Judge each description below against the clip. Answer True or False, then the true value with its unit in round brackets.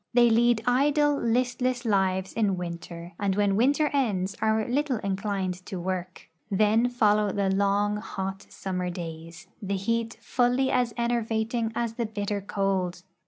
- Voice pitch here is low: False (210 Hz)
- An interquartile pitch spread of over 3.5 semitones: True (3.9 semitones)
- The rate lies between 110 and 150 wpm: True (145 wpm)